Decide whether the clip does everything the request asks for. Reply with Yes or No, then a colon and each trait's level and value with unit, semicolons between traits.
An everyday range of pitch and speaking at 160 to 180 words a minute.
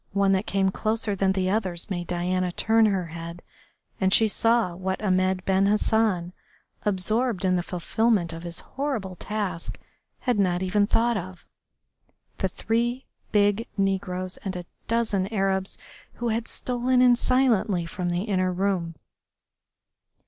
No: average, 3.3 semitones; average, 145 wpm